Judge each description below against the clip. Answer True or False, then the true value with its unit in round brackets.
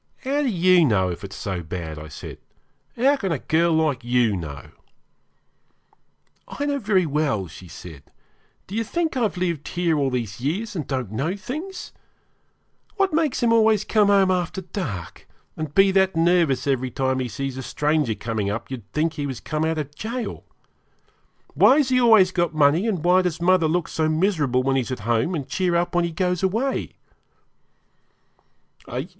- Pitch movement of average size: False (7.1 semitones)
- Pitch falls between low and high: True (160 Hz)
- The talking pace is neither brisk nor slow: True (180 wpm)